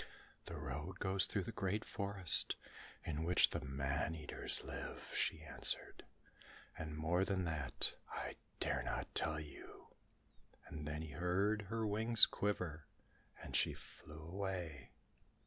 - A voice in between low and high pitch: No, very low, 85 Hz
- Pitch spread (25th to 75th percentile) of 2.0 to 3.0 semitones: No, average, 4.2 semitones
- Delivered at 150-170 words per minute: No, slow, 135 wpm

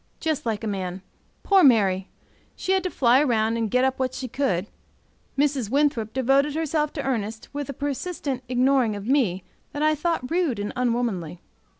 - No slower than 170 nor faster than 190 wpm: Yes, average, 180 wpm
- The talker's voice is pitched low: No, very high, 255 Hz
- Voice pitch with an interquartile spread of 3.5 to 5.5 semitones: Yes, average, 4.8 semitones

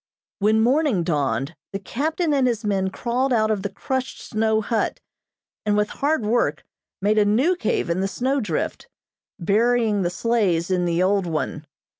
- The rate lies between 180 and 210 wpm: No, average, 170 wpm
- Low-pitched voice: No, high, 210 Hz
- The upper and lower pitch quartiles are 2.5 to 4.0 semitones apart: No, average, 4.5 semitones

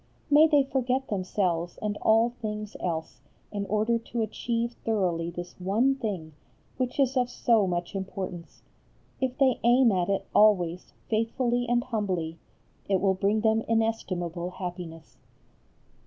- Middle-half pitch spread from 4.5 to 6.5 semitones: Yes, average, 4.9 semitones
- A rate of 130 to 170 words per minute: Yes, average, 140 wpm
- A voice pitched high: Yes, high, 210 Hz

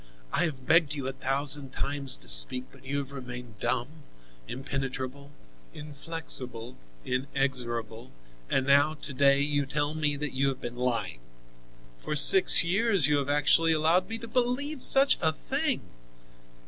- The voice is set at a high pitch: No, medium, 140 Hz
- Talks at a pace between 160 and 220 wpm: No, average, 150 wpm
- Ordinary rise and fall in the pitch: Yes, average, 3.3 semitones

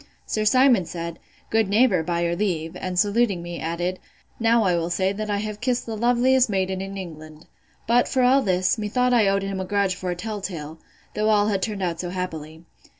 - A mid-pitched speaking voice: No, high, 195 Hz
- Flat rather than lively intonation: No, average, 3.8 semitones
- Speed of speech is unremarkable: No, fast, 210 wpm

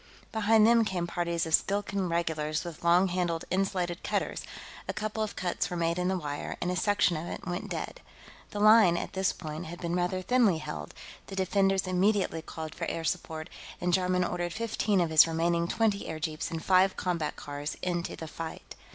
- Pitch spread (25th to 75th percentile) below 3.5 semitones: Yes, average, 2.7 semitones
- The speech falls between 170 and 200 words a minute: Yes, average, 195 wpm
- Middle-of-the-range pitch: Yes, medium, 175 Hz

